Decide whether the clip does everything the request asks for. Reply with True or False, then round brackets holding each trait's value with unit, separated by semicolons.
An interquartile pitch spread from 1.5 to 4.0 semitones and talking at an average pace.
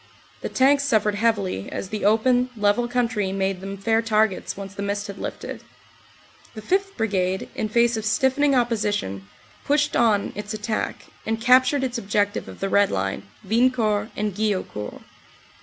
True (3.1 semitones; 160 wpm)